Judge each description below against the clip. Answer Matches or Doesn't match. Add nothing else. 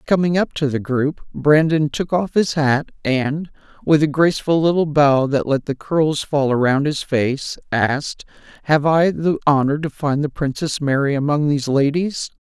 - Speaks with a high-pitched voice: Doesn't match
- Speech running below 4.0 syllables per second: Doesn't match